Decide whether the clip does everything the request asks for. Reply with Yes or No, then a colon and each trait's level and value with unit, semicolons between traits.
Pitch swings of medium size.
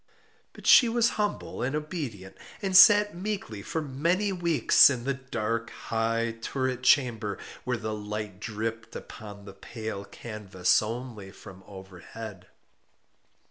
No: wide, 6.1 semitones